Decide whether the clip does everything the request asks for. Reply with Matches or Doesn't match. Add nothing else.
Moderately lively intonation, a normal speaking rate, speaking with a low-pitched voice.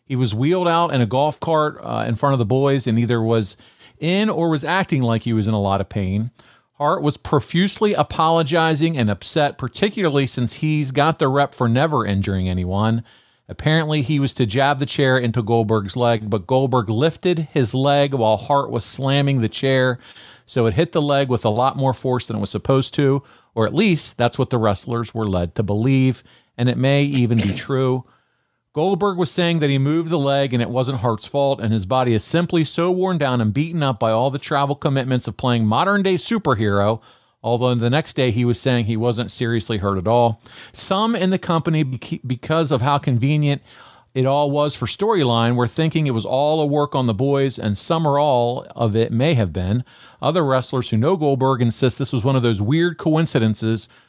Doesn't match